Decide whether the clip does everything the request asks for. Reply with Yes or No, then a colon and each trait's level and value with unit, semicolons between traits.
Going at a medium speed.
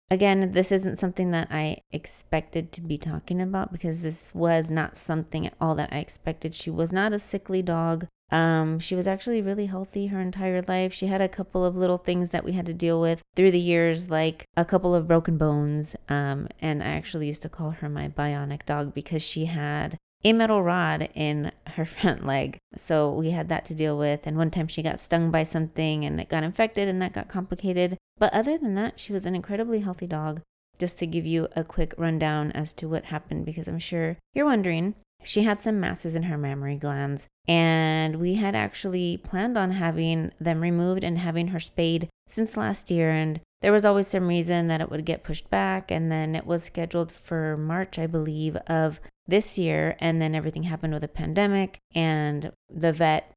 No: fast, 210 wpm